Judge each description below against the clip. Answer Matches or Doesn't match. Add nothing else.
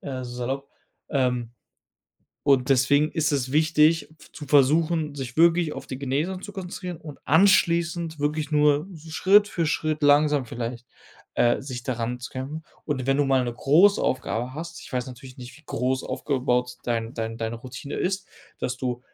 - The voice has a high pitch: Doesn't match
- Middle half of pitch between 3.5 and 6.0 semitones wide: Matches